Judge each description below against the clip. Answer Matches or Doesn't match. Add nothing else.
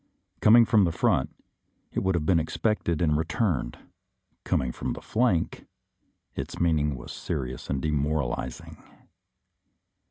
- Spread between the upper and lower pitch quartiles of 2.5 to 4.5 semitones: Doesn't match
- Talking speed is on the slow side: Matches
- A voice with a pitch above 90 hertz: Doesn't match